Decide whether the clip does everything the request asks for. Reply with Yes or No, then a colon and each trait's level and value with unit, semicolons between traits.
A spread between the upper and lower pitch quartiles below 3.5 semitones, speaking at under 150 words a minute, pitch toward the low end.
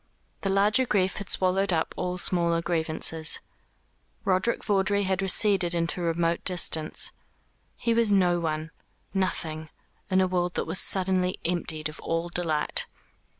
No: narrow, 2.5 semitones; average, 140 wpm; medium, 180 Hz